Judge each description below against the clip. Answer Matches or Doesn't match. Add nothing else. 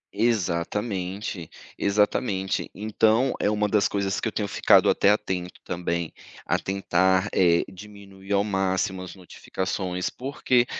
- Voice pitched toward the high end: Doesn't match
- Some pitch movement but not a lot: Doesn't match